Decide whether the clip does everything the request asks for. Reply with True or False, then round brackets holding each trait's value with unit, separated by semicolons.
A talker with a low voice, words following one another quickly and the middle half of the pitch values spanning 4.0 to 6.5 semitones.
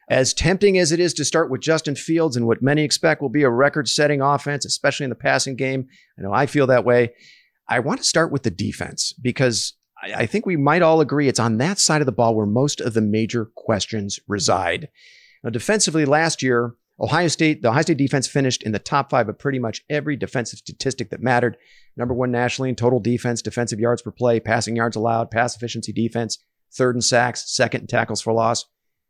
True (125 Hz; 220 wpm; 4.3 semitones)